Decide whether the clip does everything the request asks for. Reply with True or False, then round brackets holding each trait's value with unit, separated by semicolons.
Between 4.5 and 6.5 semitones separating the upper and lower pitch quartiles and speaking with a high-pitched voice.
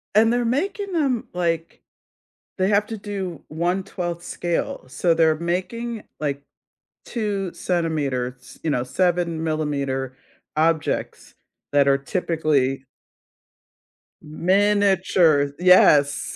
False (5.0 semitones; 170 Hz)